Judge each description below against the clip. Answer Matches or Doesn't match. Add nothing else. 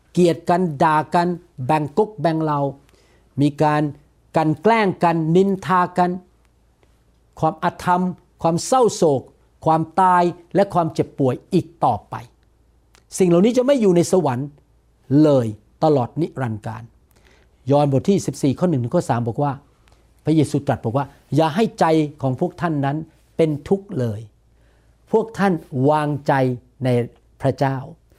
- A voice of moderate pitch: Matches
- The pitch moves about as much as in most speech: Matches